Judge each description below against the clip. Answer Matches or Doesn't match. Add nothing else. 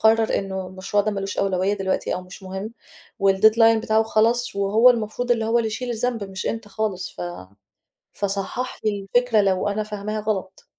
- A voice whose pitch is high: Matches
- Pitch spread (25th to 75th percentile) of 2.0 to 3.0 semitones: Matches